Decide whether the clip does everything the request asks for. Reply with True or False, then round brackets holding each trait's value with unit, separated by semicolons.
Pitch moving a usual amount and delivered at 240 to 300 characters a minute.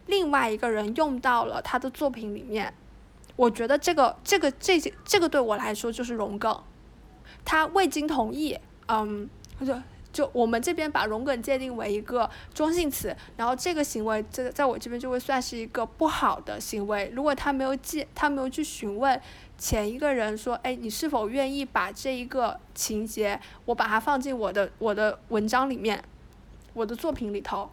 True (4.6 semitones; 275 characters per minute)